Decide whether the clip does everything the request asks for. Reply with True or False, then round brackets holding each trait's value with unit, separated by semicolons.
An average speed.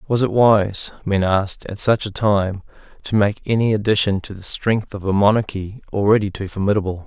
True (185 wpm)